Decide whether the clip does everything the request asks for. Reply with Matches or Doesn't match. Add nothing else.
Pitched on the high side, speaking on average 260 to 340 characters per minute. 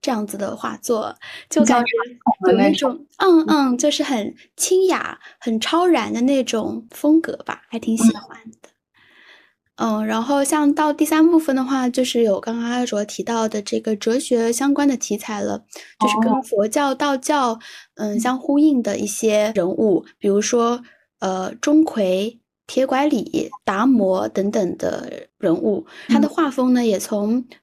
Doesn't match